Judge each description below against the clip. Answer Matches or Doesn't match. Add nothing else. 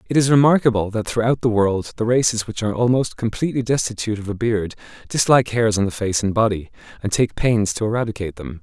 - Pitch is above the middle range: Doesn't match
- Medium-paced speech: Doesn't match